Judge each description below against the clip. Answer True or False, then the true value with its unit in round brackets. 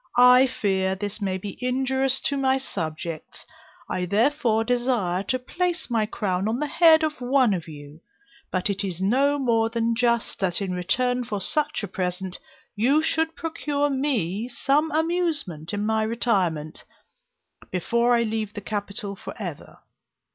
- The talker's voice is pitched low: False (225 Hz)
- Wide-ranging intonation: True (5.7 semitones)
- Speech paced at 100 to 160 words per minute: True (155 wpm)